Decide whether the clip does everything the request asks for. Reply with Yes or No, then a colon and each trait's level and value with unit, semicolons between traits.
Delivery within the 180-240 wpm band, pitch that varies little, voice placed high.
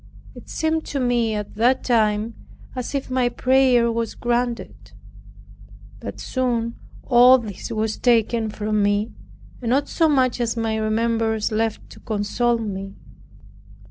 No: average, 140 wpm; narrow, 2.3 semitones; high, 230 Hz